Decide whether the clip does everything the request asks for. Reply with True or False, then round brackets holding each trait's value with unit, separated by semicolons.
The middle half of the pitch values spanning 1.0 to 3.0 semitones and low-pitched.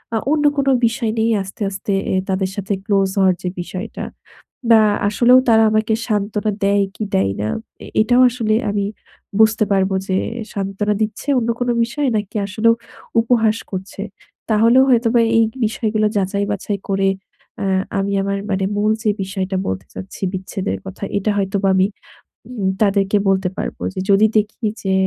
False (2.5 semitones; 205 Hz)